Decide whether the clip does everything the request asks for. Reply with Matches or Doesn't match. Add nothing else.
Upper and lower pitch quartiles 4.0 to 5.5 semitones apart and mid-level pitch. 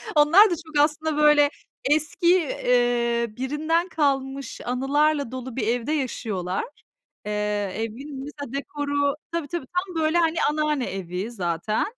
Doesn't match